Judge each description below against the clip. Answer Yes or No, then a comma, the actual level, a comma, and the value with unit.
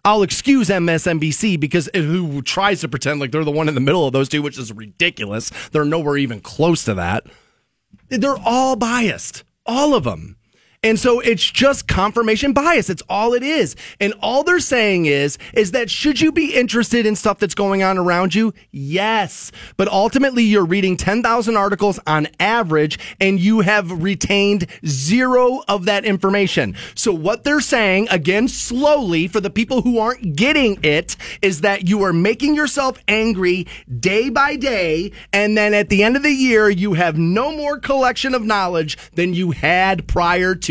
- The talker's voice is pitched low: No, high, 200 Hz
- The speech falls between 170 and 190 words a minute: Yes, average, 180 wpm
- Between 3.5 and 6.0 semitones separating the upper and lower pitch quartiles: Yes, wide, 5.5 semitones